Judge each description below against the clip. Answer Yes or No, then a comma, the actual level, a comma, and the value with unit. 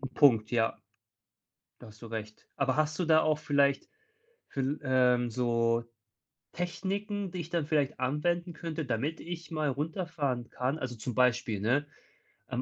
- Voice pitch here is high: No, medium, 140 Hz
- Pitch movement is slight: No, average, 4.7 semitones